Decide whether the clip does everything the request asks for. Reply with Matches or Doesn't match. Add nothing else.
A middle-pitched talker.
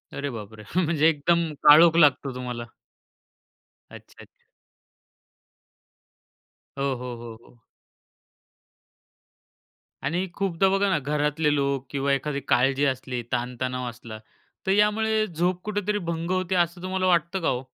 Matches